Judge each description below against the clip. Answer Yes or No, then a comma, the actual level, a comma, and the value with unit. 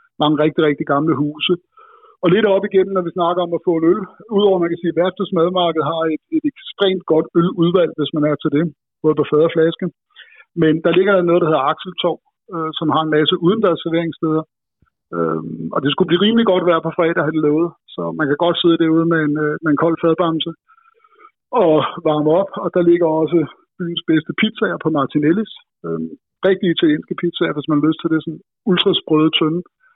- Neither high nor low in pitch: Yes, medium, 165 Hz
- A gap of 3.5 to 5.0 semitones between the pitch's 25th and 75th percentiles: No, average, 2.8 semitones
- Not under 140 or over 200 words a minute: No, average, 210 wpm